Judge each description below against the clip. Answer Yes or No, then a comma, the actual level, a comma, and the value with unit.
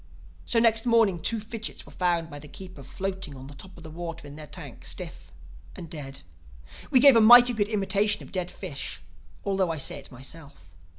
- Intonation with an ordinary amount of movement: No, wide, 6.5 semitones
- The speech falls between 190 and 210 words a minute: Yes, average, 195 wpm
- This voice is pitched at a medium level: Yes, medium, 180 Hz